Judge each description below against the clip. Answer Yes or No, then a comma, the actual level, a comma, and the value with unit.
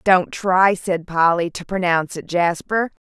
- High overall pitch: No, medium, 180 Hz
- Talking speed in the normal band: Yes, average, 155 wpm